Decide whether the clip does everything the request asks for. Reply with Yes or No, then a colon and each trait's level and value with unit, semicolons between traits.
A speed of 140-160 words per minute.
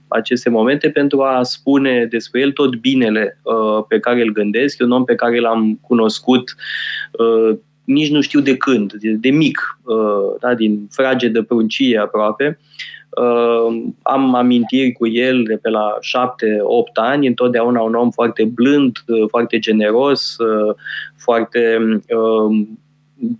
Yes: average, 150 wpm